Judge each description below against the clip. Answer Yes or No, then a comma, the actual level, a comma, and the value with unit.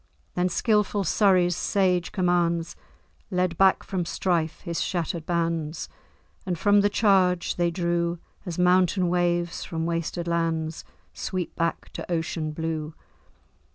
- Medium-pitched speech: Yes, medium, 175 Hz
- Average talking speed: No, slow, 125 wpm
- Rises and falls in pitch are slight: Yes, narrow, 1.6 semitones